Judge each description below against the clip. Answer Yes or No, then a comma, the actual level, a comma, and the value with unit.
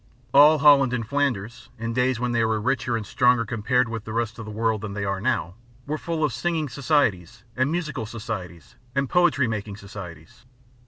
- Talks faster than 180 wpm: Yes, average, 195 wpm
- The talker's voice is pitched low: Yes, low, 115 Hz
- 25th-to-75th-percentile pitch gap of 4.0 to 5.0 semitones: Yes, average, 4.5 semitones